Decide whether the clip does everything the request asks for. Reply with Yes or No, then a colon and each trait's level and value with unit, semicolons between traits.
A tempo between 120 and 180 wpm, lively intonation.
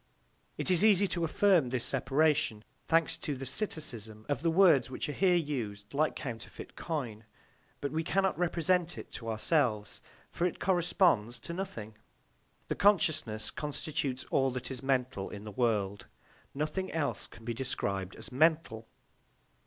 Yes: average, 155 wpm; wide, 6.6 semitones